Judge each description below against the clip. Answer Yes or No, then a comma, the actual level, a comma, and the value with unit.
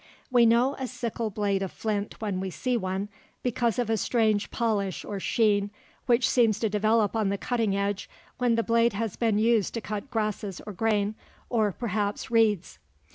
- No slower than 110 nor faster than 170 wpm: No, average, 185 wpm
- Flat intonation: Yes, narrow, 2.3 semitones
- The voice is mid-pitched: No, high, 215 Hz